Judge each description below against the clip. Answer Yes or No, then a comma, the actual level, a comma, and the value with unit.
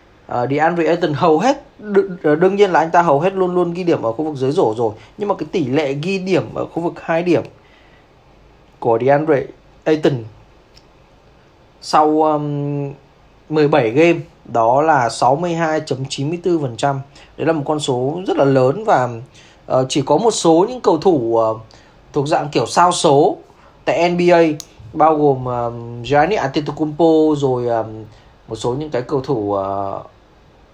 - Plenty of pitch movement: No, average, 4.3 semitones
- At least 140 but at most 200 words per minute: Yes, slow, 165 wpm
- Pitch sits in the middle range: Yes, medium, 150 Hz